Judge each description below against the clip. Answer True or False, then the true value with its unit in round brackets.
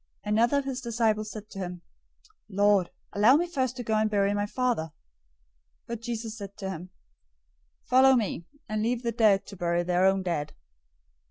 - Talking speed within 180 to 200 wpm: True (185 wpm)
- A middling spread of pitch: True (3.6 semitones)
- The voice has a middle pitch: False (215 Hz)